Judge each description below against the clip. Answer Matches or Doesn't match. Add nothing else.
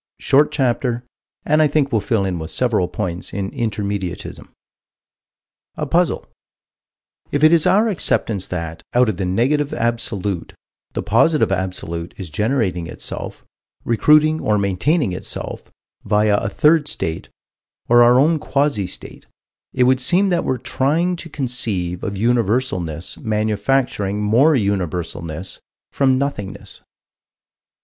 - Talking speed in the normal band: Doesn't match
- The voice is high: Doesn't match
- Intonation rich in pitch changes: Matches